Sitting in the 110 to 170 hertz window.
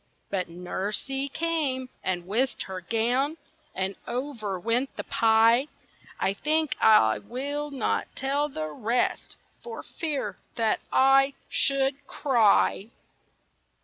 No: very high, 250 Hz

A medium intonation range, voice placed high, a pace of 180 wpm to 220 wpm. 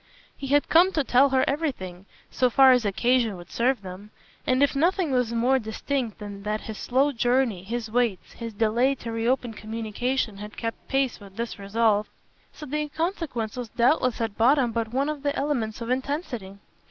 Yes: average, 3.8 semitones; high, 240 Hz; average, 185 wpm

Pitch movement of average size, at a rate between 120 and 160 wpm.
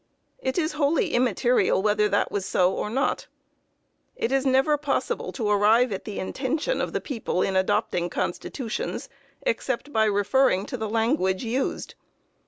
Yes: average, 4.8 semitones; average, 155 wpm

